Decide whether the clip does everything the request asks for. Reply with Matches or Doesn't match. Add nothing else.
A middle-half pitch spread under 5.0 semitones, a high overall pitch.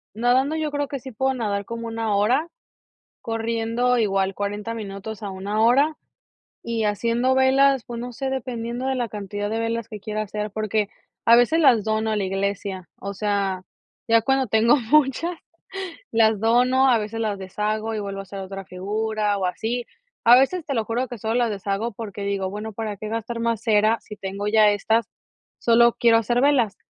Matches